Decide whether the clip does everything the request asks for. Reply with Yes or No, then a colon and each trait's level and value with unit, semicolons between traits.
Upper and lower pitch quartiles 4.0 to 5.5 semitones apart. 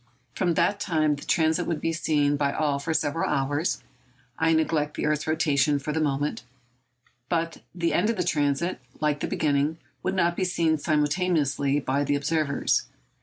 No: narrow, 2.5 semitones